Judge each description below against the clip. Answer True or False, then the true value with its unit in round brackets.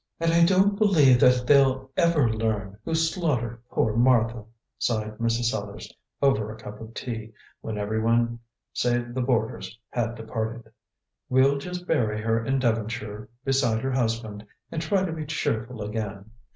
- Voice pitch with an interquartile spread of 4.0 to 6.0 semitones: False (3.5 semitones)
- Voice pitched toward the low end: True (120 Hz)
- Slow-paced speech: False (150 wpm)